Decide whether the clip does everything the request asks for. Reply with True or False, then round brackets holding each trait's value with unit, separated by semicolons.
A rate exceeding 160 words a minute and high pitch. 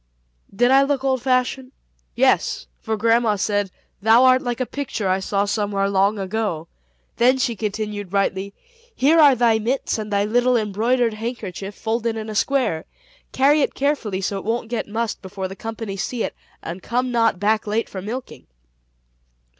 True (170 wpm; 220 Hz)